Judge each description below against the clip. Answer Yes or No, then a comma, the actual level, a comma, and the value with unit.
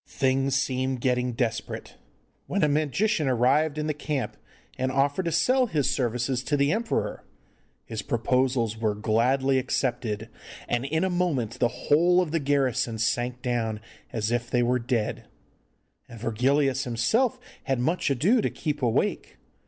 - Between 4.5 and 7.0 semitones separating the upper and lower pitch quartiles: No, average, 3.7 semitones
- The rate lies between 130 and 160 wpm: Yes, average, 150 wpm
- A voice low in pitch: Yes, low, 130 Hz